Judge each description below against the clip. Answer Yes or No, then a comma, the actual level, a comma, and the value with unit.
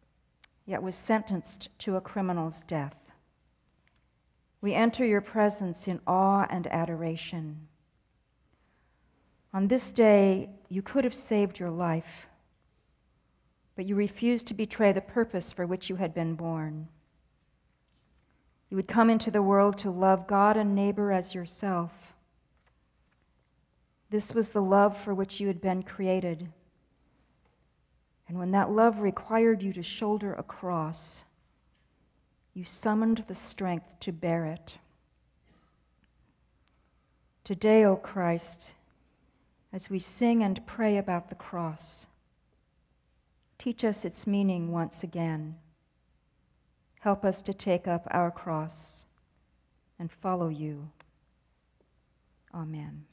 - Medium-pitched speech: Yes, medium, 180 Hz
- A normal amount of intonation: Yes, average, 4.2 semitones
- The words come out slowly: Yes, slow, 120 wpm